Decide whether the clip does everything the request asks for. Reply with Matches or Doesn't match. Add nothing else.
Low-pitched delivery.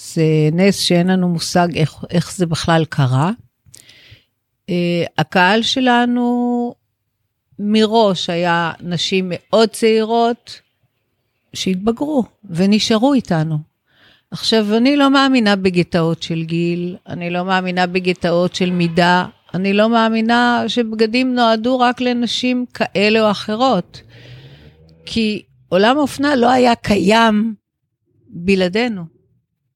Doesn't match